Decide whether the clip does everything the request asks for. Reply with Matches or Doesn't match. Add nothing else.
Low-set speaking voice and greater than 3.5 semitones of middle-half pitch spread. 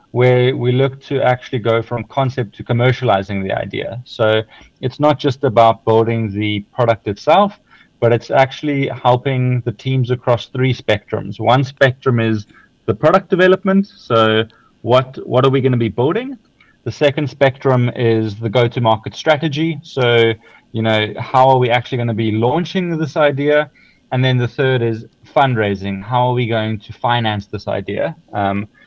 Doesn't match